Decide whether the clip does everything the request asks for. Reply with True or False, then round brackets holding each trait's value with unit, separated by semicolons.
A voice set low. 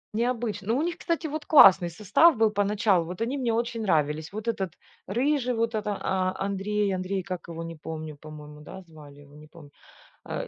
False (195 Hz)